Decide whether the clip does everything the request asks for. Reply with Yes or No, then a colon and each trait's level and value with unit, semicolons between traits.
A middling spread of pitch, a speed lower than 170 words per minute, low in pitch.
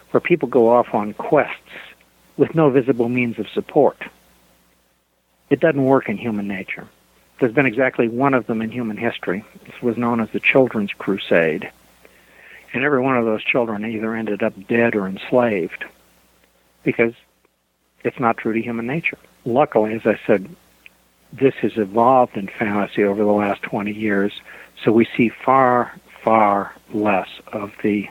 Yes: average, 3.6 semitones; average, 160 wpm; low, 110 Hz